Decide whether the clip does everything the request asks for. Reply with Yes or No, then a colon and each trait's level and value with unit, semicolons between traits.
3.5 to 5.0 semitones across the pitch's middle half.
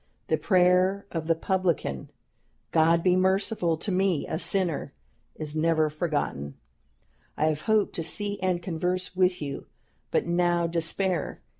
No: average, 2.8 semitones